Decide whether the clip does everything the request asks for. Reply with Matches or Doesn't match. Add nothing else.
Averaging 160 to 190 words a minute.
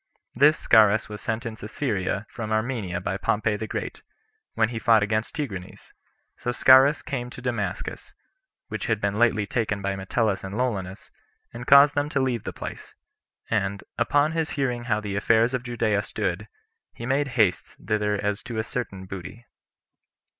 Matches